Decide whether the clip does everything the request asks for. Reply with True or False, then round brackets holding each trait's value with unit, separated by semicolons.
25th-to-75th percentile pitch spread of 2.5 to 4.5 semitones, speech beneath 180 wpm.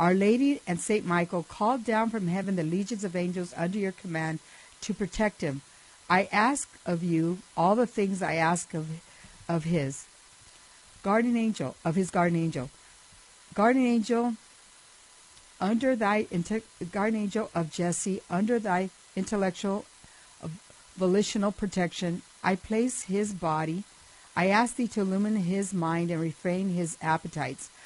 True (3.8 semitones; 140 wpm)